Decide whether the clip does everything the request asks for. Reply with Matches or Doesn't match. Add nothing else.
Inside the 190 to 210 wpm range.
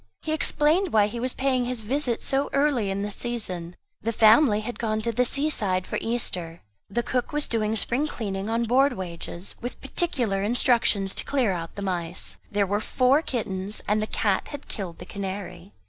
Matches